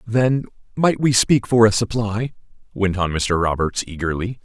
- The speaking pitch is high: No, low, 105 Hz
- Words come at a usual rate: Yes, average, 160 wpm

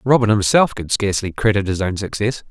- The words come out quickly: No, average, 190 wpm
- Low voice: Yes, low, 105 Hz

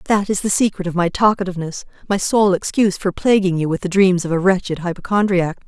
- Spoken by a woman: Yes, female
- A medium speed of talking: No, fast, 210 wpm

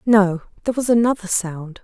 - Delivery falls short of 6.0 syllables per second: Yes, 5.4 syllables/s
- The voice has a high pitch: Yes, high, 205 Hz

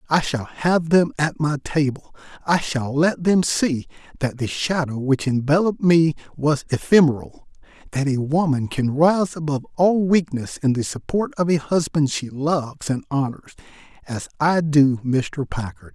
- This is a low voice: No, medium, 150 Hz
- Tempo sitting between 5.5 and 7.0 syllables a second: No, 4.5 syllables/s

